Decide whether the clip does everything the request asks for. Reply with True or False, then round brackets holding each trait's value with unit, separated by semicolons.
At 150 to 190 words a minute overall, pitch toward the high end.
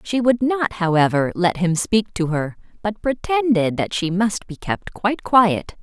True (185 wpm; 200 Hz)